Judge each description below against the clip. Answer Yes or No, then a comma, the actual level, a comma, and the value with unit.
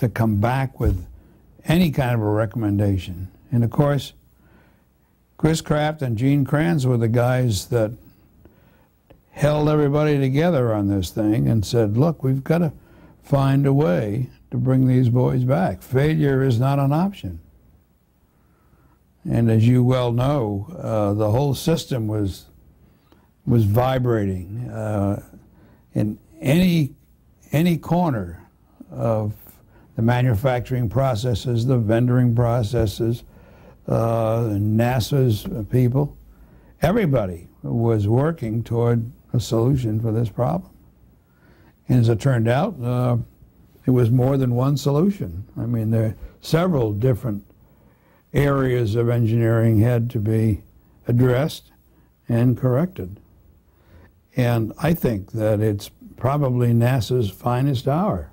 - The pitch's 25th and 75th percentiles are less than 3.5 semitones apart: No, average, 3.8 semitones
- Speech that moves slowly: Yes, slow, 120 wpm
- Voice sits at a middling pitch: No, low, 120 Hz